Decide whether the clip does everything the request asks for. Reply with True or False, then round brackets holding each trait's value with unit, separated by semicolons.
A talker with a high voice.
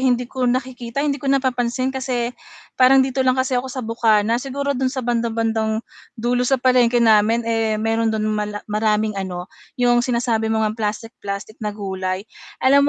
True (235 Hz)